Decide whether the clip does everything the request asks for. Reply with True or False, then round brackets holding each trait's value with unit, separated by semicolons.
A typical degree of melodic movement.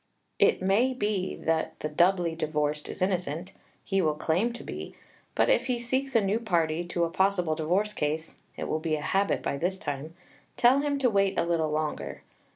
True (4.7 semitones)